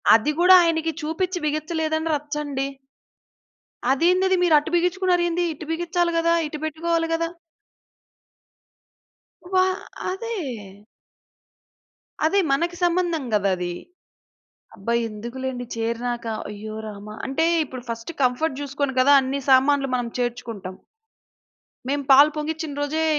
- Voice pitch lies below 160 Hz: No, very high, 300 Hz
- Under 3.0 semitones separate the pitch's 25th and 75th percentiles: No, average, 5.1 semitones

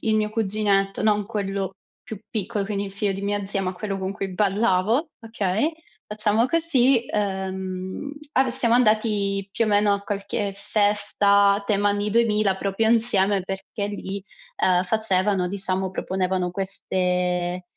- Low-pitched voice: No, high, 200 Hz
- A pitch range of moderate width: No, narrow, 1.9 semitones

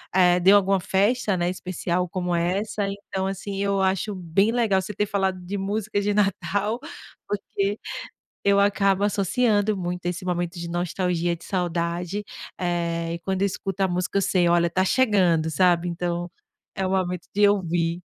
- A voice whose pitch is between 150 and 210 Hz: Yes, medium, 185 Hz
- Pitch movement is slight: Yes, narrow, 2.3 semitones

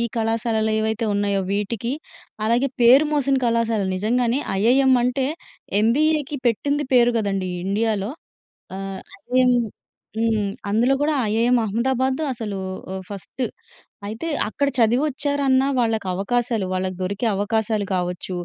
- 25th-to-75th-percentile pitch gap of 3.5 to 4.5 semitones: Yes, average, 3.8 semitones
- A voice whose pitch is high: Yes, high, 230 Hz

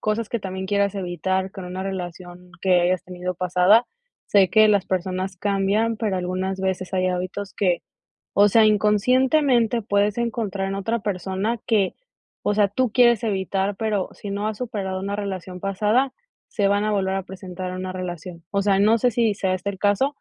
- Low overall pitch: No, high, 195 Hz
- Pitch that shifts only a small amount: Yes, narrow, 2.3 semitones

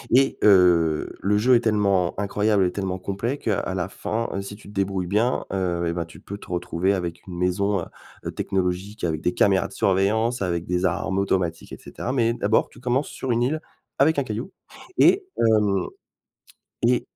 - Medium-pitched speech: No, low, 100 Hz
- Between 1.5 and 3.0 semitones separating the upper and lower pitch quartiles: No, average, 3.5 semitones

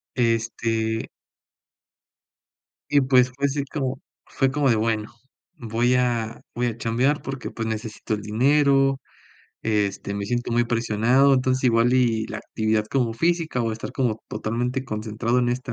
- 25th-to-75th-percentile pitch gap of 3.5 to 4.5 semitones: No, average, 2.7 semitones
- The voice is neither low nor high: No, low, 120 Hz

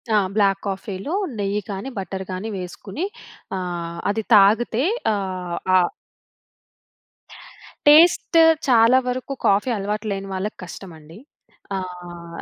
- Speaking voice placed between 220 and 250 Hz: No, high, 195 Hz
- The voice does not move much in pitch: No, average, 3.1 semitones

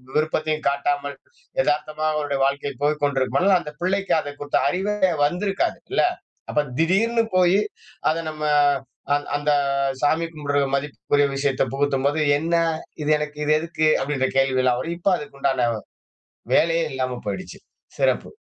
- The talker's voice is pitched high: No, medium, 150 Hz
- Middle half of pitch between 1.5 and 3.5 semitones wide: Yes, average, 2.9 semitones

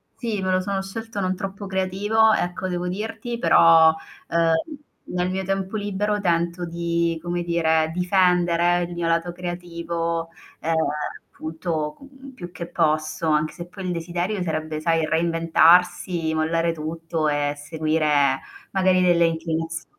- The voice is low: No, medium, 170 Hz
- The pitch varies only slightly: Yes, narrow, 2.3 semitones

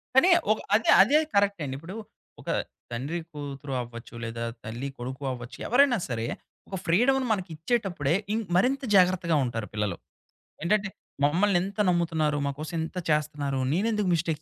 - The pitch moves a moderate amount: No, wide, 6.7 semitones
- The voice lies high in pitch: No, medium, 165 Hz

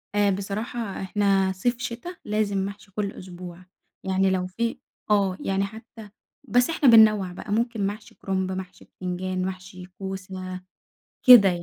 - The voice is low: No, high, 195 Hz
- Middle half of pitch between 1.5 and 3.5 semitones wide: Yes, narrow, 2.4 semitones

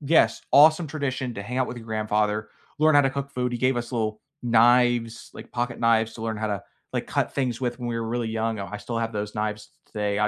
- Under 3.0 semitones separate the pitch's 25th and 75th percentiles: Yes, narrow, 2.6 semitones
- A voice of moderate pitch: No, low, 115 Hz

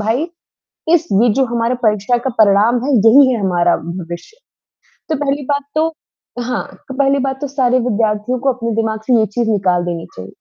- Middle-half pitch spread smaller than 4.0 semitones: No, average, 4.7 semitones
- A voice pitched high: Yes, high, 235 Hz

